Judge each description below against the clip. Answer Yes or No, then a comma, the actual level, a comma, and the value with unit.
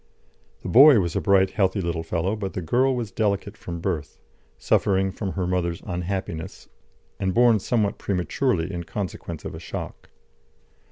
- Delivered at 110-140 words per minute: No, average, 165 wpm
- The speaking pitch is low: Yes, very low, 95 Hz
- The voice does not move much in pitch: No, average, 3.2 semitones